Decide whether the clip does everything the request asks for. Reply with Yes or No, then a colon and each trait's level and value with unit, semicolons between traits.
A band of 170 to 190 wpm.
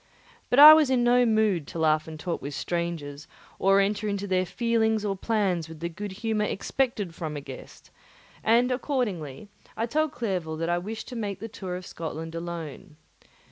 Yes: average, 185 wpm